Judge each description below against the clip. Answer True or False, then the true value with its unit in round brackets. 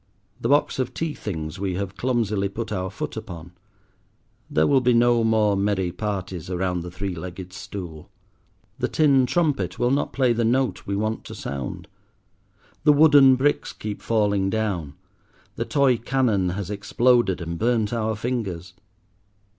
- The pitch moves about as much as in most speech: True (5.0 semitones)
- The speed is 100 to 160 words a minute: True (155 wpm)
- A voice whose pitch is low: True (105 Hz)